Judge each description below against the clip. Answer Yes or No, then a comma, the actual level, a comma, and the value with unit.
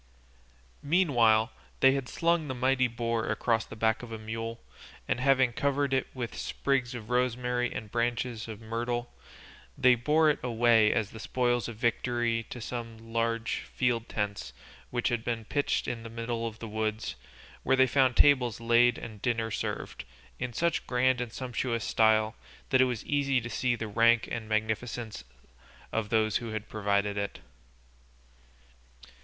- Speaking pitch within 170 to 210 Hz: No, low, 120 Hz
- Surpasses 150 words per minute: Yes, average, 165 wpm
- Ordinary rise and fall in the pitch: No, narrow, 2.0 semitones